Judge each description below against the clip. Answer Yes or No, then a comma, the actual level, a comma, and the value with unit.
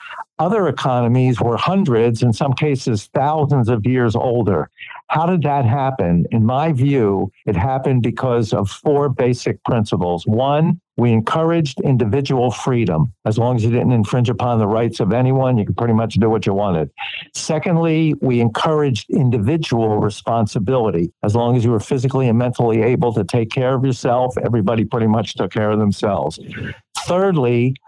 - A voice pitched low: Yes, low, 120 Hz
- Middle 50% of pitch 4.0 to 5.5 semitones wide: No, average, 3.5 semitones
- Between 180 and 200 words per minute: No, average, 165 wpm